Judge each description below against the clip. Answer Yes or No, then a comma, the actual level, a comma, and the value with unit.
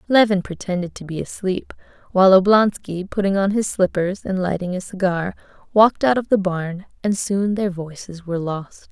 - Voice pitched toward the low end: No, high, 190 Hz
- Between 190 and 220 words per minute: No, average, 175 wpm